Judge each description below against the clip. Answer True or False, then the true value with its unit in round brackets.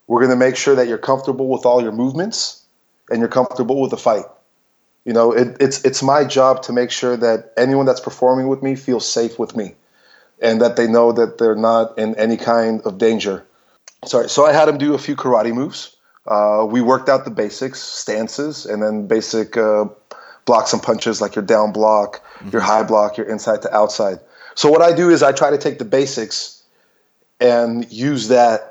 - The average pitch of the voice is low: True (120 Hz)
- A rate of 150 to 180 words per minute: False (205 wpm)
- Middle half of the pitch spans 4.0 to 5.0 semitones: False (3.2 semitones)